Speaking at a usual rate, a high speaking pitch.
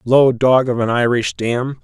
No: average, 195 wpm; low, 125 Hz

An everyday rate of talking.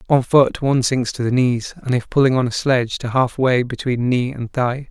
No: fast, 235 wpm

